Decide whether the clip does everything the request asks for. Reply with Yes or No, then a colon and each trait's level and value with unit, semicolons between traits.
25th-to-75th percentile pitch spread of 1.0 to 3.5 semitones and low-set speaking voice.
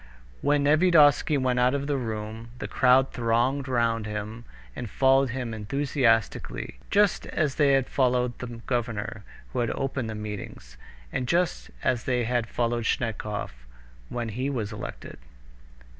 Yes: average, 3.2 semitones; low, 125 Hz